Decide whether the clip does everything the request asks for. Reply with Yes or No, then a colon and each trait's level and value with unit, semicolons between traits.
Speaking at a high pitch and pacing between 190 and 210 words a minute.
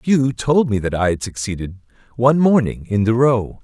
No: low, 115 Hz; average, 200 wpm